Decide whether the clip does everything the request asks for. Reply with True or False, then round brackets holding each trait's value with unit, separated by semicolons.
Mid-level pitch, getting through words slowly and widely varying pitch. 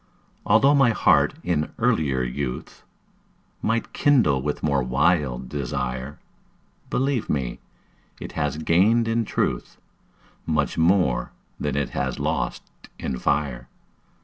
False (75 Hz; 115 wpm; 7.5 semitones)